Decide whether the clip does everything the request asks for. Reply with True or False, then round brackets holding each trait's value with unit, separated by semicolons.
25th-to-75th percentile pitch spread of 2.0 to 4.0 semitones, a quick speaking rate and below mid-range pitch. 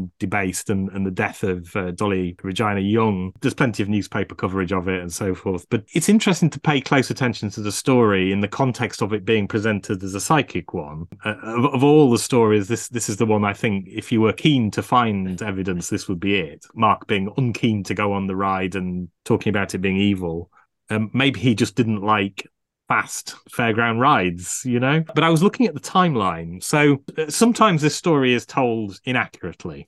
False (4.7 semitones; 210 wpm; 110 Hz)